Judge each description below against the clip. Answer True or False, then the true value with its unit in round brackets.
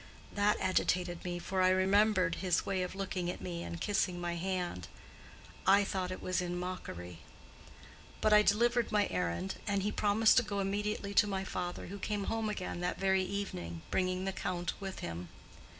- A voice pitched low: False (185 Hz)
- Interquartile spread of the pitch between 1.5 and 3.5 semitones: True (2.4 semitones)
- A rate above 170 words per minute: True (180 wpm)